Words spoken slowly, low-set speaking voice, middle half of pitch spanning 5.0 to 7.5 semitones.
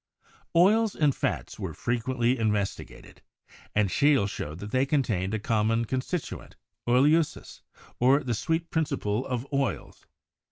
Yes: slow, 125 wpm; low, 125 Hz; average, 5.3 semitones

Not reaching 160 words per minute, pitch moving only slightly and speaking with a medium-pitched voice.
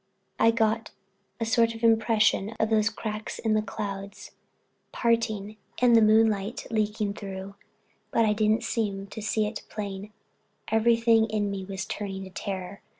No: average, 150 wpm; narrow, 2.1 semitones; high, 215 Hz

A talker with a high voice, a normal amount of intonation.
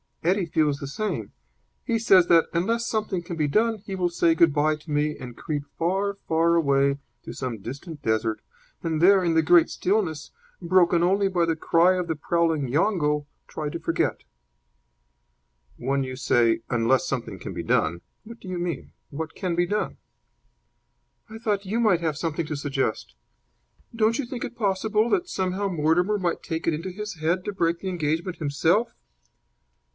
No: medium, 170 Hz; average, 4.4 semitones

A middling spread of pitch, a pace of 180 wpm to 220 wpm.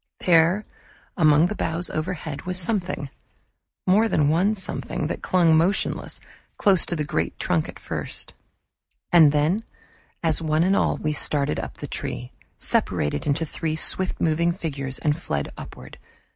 No: average, 3.3 semitones; average, 150 wpm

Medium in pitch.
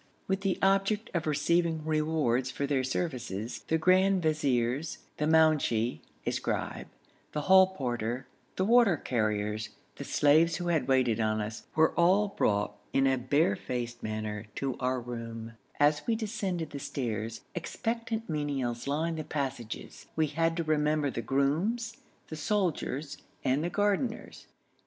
Yes: medium, 150 Hz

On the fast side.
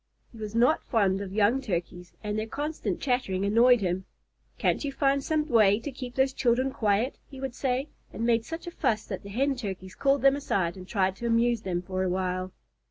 Yes: fast, 215 wpm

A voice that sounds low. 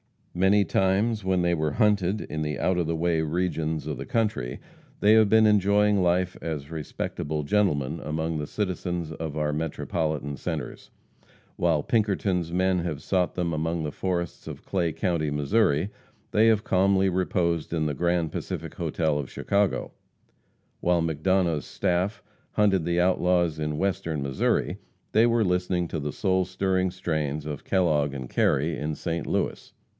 Yes: very low, 85 Hz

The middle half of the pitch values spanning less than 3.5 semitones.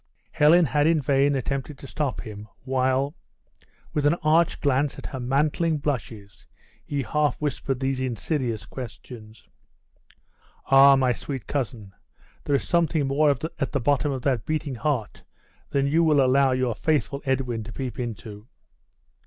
Yes: average, 2.8 semitones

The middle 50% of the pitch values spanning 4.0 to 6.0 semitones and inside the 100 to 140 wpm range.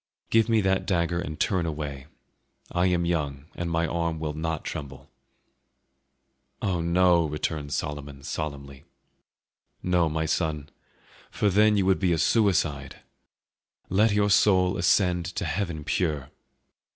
No: average, 3.5 semitones; slow, 135 wpm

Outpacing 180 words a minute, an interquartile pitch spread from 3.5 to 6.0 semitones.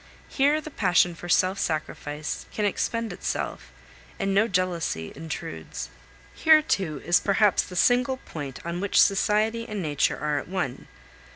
No: average, 150 wpm; wide, 5.5 semitones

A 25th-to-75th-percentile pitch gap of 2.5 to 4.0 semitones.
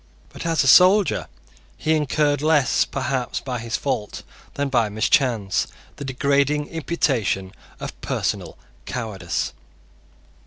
No: average, 4.4 semitones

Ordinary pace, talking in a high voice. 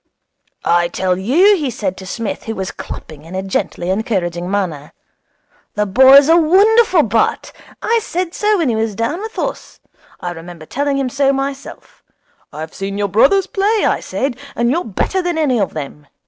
Yes: average, 180 wpm; high, 230 Hz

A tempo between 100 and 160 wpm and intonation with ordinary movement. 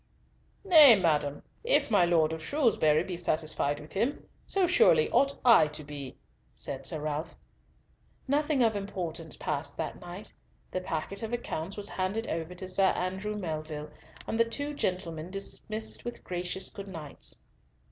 No: average, 155 wpm; wide, 6.1 semitones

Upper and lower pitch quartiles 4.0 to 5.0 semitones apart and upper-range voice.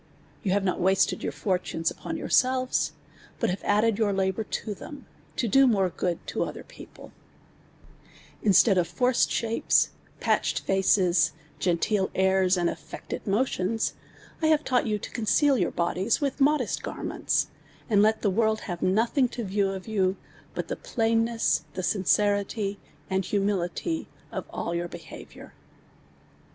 No: average, 3.5 semitones; high, 205 Hz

